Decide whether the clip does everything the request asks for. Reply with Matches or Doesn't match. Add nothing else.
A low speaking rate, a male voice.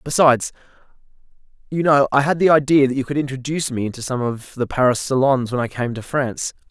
Doesn't match